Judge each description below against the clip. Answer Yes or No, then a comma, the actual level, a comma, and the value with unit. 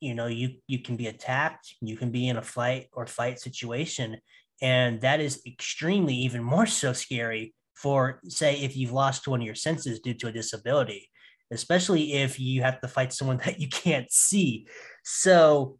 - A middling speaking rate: Yes, average, 185 wpm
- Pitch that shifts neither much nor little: Yes, average, 3.1 semitones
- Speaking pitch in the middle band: No, low, 130 Hz